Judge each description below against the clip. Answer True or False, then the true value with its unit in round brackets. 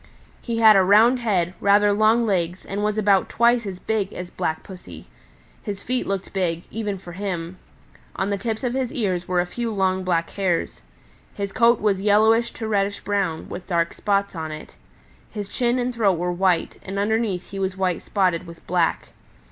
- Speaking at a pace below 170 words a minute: False (190 wpm)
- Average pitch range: True (3.3 semitones)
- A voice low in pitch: False (195 Hz)